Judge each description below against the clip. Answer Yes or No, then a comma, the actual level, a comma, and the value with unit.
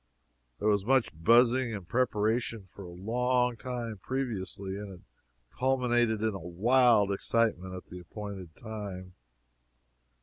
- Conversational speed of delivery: No, slow, 130 wpm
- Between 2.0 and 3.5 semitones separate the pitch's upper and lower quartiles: No, average, 4.3 semitones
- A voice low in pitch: Yes, low, 110 Hz